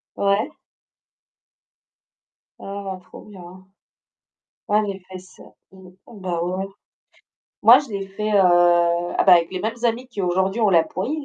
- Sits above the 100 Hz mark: Yes, high, 190 Hz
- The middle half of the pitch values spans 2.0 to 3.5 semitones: Yes, narrow, 2.5 semitones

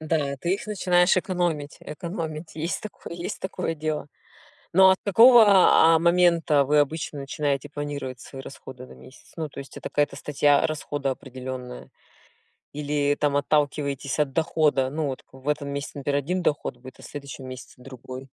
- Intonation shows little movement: No, average, 3.2 semitones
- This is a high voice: No, medium, 145 Hz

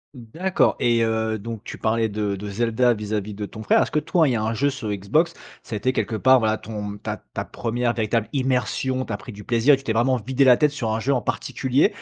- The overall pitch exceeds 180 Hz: No, low, 115 Hz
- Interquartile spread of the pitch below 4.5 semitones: Yes, average, 3.3 semitones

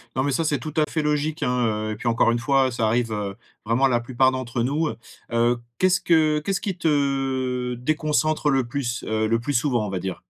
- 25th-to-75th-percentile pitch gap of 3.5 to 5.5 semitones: Yes, average, 4.2 semitones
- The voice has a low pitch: Yes, low, 130 Hz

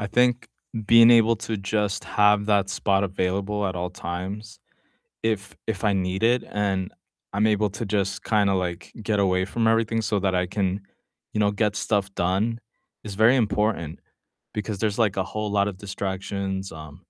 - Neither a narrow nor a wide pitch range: No, narrow, 2.0 semitones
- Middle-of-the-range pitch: No, low, 100 Hz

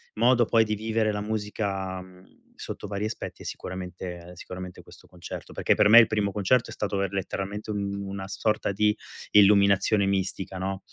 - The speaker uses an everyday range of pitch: No, narrow, 2.0 semitones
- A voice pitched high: No, low, 100 Hz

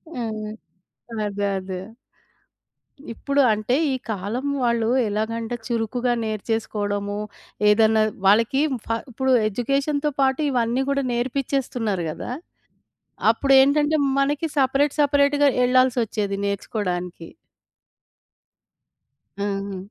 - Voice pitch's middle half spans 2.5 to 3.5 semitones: No, average, 4.6 semitones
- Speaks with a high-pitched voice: Yes, high, 230 Hz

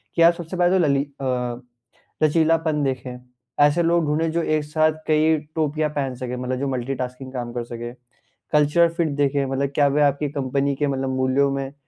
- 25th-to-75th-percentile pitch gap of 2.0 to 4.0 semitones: Yes, average, 3.2 semitones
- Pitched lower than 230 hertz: Yes, medium, 140 Hz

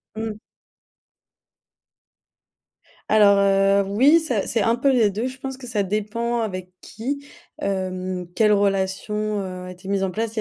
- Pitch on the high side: Yes, high, 210 Hz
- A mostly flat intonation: No, average, 3.1 semitones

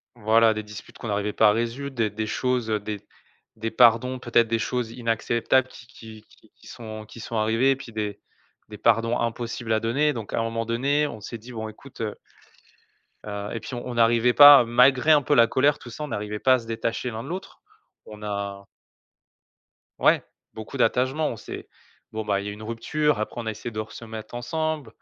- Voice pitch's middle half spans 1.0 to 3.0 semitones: Yes, narrow, 2.6 semitones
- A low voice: Yes, low, 115 Hz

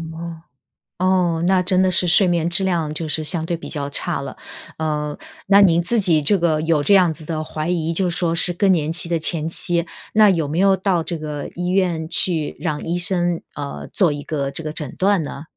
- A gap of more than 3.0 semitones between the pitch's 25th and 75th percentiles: No, narrow, 2.5 semitones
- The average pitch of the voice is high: No, medium, 170 Hz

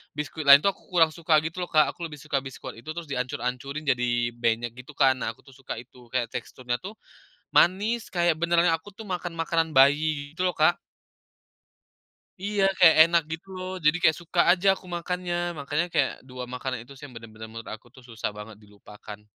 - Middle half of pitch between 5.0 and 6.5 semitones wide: Yes, wide, 5.4 semitones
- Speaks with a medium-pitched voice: Yes, medium, 150 Hz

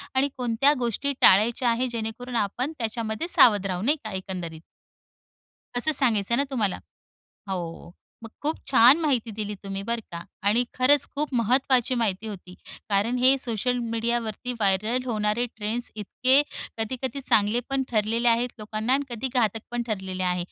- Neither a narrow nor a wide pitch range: Yes, average, 3.3 semitones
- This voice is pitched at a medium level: No, high, 230 Hz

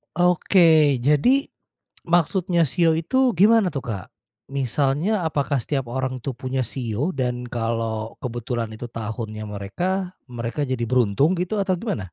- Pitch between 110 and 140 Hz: Yes, low, 135 Hz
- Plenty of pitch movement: Yes, wide, 6.9 semitones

